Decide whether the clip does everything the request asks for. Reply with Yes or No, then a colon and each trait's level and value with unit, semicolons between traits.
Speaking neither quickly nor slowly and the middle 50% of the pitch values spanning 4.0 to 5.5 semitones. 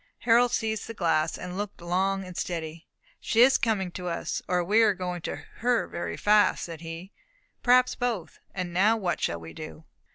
Yes: average, 190 wpm; average, 4.4 semitones